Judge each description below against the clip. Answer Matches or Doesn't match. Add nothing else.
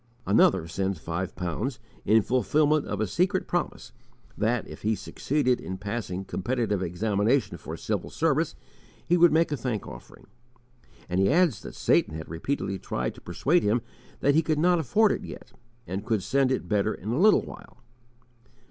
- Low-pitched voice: Matches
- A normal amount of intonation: Doesn't match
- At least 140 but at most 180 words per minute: Matches